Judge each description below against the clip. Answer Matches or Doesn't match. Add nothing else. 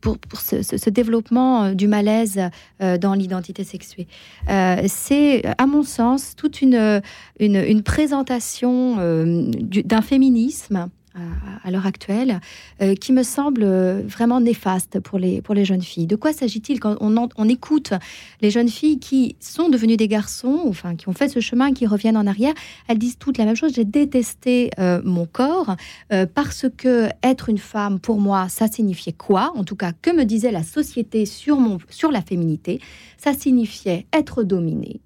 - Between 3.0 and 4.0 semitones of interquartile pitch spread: Doesn't match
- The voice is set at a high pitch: Matches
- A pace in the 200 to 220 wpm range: Doesn't match